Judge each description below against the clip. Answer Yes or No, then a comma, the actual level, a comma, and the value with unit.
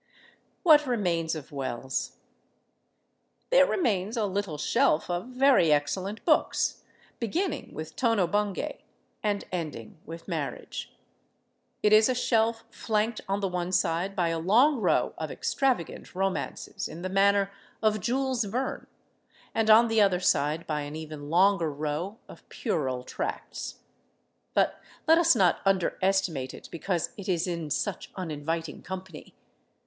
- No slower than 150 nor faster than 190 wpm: No, average, 140 wpm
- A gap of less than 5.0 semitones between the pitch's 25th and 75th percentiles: No, average, 5.3 semitones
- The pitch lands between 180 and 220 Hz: Yes, high, 190 Hz